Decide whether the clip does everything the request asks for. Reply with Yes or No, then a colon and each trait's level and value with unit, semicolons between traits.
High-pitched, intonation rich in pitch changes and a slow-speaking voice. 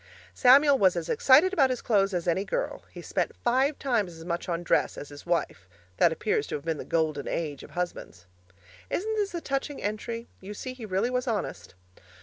No: high, 205 Hz; wide, 7.7 semitones; fast, 205 wpm